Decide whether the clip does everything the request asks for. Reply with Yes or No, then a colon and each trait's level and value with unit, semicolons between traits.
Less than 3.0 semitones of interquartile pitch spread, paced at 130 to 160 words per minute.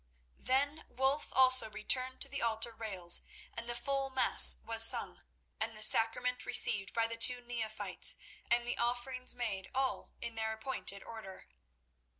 Yes: narrow, 2.5 semitones; average, 155 wpm